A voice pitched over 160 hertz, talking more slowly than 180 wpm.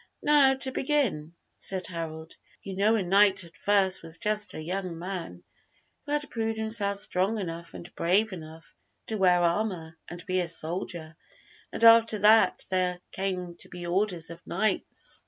Yes: medium, 185 Hz; average, 165 wpm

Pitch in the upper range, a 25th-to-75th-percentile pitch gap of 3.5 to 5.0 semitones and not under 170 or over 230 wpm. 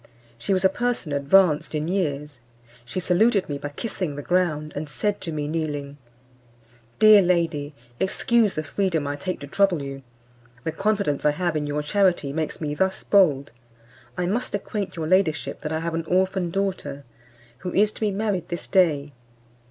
No: medium, 170 Hz; average, 4.6 semitones; average, 175 wpm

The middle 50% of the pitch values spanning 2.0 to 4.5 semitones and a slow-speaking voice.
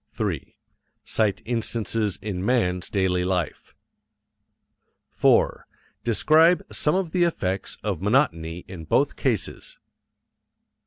No: wide, 5.4 semitones; slow, 100 wpm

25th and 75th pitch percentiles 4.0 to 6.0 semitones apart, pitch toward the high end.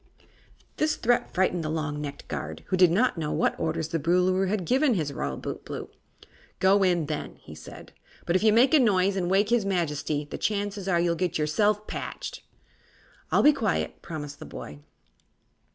No: average, 4.7 semitones; medium, 180 Hz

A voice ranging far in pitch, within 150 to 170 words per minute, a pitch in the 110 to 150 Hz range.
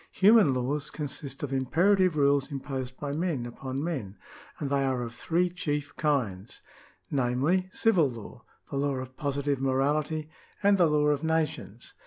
No: average, 3.3 semitones; average, 160 wpm; medium, 140 Hz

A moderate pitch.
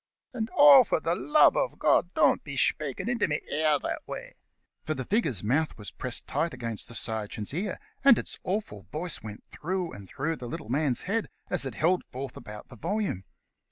Yes: medium, 155 Hz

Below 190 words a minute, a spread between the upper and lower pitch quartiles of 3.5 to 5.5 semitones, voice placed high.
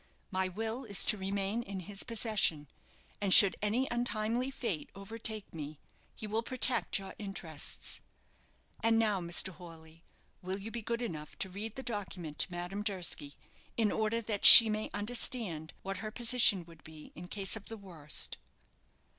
Yes: average, 165 wpm; average, 4.1 semitones; high, 200 Hz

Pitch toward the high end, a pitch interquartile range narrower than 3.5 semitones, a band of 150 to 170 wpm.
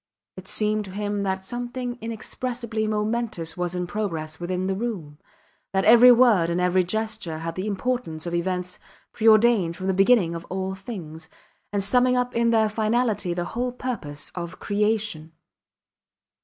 No: high, 200 Hz; average, 4.5 semitones; average, 155 wpm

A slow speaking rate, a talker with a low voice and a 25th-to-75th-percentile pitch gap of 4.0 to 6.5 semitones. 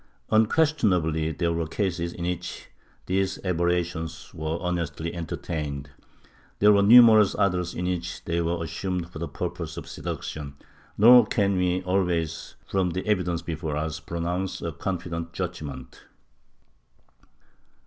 No: slow, 130 wpm; very low, 85 Hz; narrow, 2.4 semitones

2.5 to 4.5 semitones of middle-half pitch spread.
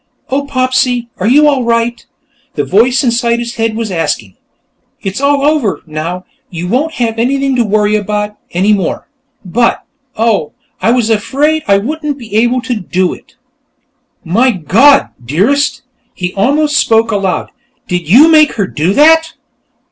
No: wide, 5.6 semitones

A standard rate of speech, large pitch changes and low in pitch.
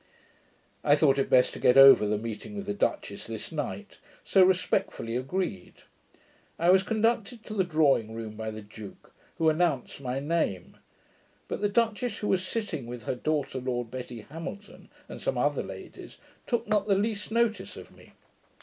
No: average, 175 wpm; wide, 8.7 semitones; medium, 160 Hz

